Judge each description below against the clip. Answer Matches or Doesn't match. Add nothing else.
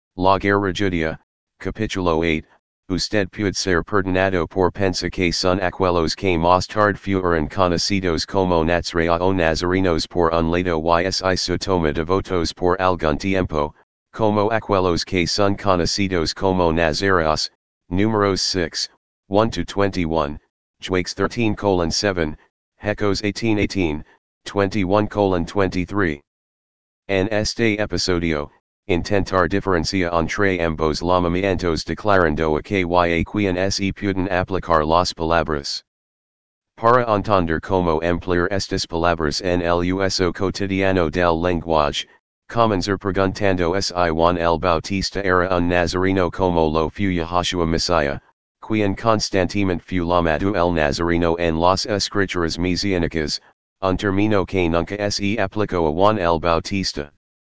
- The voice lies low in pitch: Matches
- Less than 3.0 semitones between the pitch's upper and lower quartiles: Matches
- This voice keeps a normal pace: Doesn't match